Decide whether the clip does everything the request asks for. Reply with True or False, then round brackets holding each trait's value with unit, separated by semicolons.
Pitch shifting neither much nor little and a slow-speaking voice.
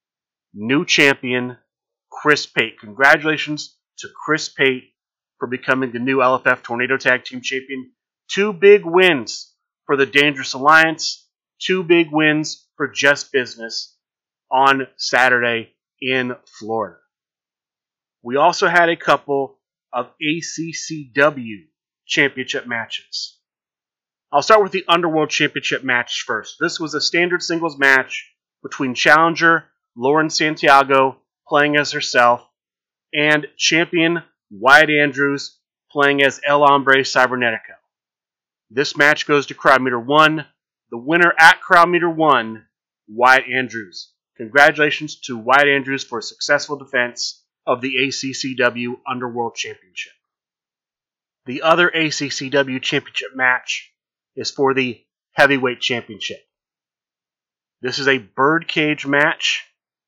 True (3.3 semitones; 115 wpm)